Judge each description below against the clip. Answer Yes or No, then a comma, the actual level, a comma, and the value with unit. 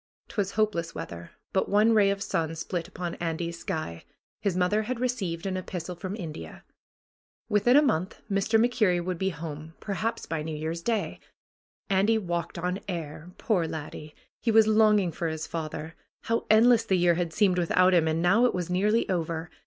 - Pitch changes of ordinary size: Yes, average, 4.2 semitones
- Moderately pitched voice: Yes, medium, 180 Hz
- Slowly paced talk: No, average, 185 wpm